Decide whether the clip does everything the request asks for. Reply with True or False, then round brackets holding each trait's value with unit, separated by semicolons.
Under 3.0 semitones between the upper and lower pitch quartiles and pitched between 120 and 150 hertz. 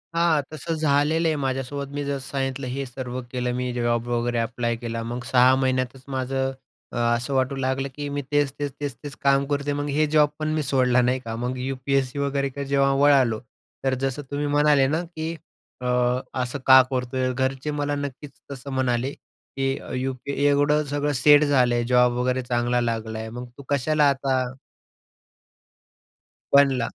True (2.4 semitones; 135 Hz)